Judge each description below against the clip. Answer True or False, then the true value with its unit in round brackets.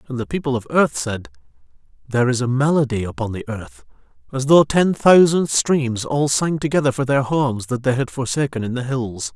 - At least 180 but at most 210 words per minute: True (200 wpm)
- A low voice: True (130 Hz)